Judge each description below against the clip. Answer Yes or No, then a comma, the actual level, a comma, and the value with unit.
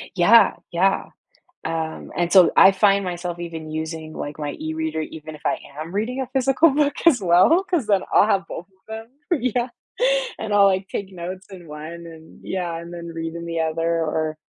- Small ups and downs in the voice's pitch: No, average, 3.7 semitones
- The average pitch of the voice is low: No, medium, 175 Hz